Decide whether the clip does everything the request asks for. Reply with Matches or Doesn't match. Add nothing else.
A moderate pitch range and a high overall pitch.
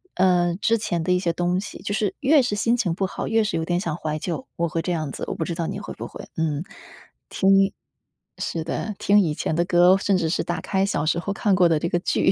Doesn't match